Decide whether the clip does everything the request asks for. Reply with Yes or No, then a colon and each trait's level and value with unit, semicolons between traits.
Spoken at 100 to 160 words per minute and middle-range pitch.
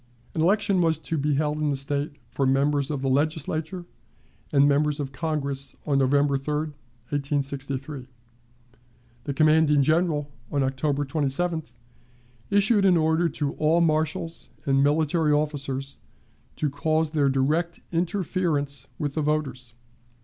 Yes: slow, 135 wpm; medium, 150 Hz